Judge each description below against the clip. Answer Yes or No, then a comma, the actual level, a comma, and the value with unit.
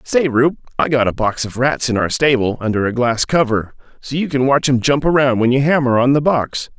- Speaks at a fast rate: Yes, fast, 250 wpm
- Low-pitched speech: Yes, low, 130 Hz